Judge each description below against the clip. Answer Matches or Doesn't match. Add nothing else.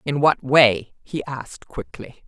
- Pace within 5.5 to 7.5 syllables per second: Doesn't match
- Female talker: Matches